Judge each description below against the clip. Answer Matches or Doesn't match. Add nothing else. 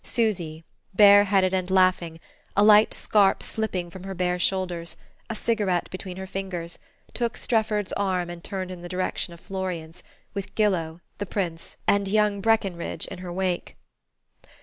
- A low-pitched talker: Doesn't match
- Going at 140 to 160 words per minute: Matches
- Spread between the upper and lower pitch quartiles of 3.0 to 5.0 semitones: Doesn't match